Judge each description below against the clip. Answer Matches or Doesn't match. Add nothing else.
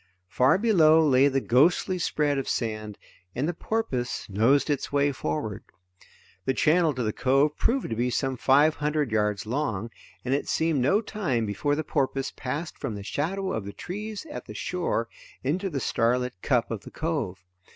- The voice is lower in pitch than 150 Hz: Matches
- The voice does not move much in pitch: Doesn't match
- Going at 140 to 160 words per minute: Doesn't match